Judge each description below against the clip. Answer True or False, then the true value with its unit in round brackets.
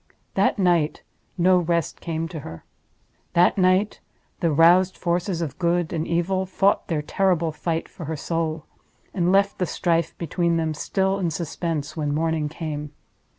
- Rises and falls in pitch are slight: True (2.3 semitones)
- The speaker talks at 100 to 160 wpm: True (150 wpm)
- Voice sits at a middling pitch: True (170 Hz)